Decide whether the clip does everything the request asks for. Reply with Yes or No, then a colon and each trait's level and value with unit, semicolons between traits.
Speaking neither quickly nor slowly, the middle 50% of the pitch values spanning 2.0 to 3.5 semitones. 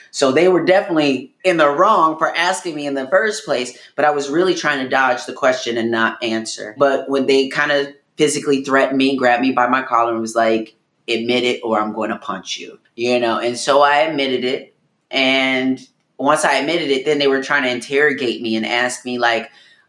No: fast, 220 wpm; average, 3.1 semitones